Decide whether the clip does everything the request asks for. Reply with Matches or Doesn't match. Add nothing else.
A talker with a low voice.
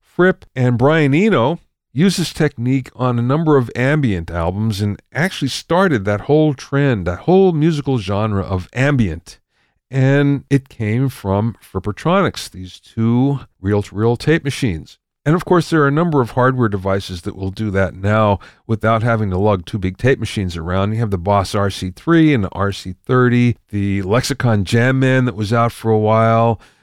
Matches